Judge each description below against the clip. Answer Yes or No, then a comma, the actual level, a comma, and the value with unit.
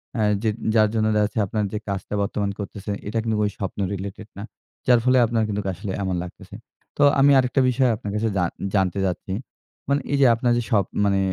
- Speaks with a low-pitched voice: Yes, low, 105 Hz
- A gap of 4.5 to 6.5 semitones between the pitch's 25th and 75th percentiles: No, average, 2.9 semitones